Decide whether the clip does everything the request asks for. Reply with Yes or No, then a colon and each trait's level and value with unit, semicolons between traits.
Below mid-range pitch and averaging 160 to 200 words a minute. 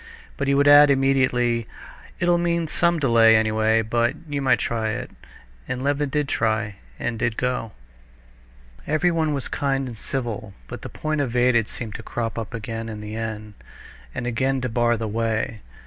Yes: low, 120 Hz; average, 170 wpm